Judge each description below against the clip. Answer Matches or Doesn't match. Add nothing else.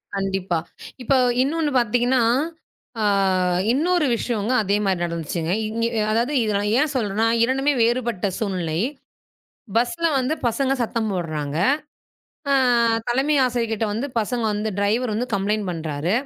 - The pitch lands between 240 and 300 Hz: Doesn't match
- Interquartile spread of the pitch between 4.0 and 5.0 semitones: Matches